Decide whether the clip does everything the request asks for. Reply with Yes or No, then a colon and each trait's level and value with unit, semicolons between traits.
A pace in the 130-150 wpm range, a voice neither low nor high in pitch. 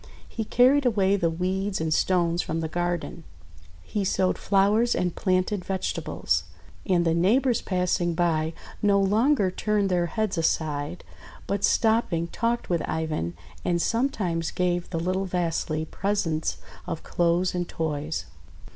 Yes: average, 140 wpm; medium, 180 Hz